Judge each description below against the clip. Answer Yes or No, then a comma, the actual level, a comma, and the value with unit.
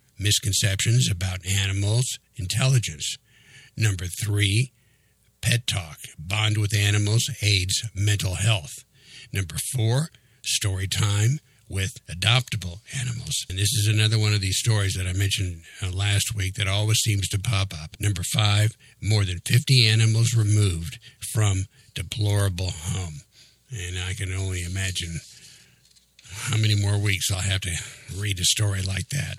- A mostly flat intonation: No, average, 3.3 semitones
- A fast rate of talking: No, slow, 135 wpm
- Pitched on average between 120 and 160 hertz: No, low, 105 Hz